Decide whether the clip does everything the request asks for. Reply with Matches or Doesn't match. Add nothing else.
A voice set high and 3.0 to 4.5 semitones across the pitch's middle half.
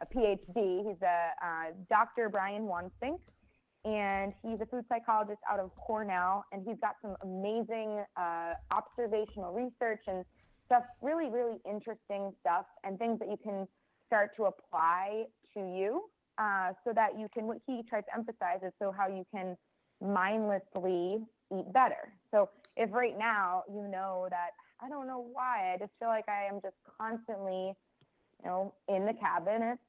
Matches